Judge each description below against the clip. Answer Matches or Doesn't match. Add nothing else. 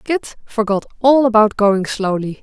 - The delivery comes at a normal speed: Matches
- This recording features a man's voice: Doesn't match